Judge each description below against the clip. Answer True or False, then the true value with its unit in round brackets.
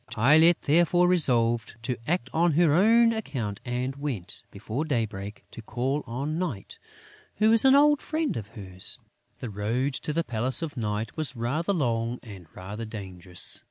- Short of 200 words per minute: True (160 wpm)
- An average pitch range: False (7.1 semitones)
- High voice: False (125 Hz)